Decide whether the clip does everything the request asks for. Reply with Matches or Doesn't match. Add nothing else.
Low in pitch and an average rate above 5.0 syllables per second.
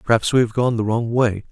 Matches